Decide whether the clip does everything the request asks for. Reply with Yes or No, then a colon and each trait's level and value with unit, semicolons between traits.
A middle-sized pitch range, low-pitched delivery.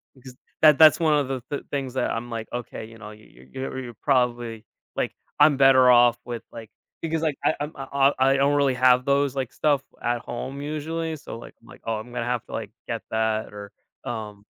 Yes: average, 3.3 semitones; low, 130 Hz